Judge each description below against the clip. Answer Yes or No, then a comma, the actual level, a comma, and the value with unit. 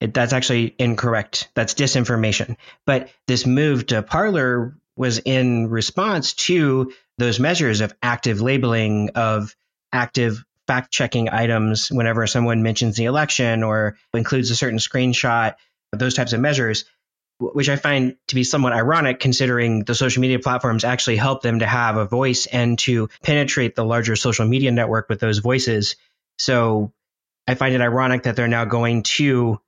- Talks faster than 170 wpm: No, average, 155 wpm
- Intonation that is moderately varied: No, narrow, 2.1 semitones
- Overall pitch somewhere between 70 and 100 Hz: No, low, 120 Hz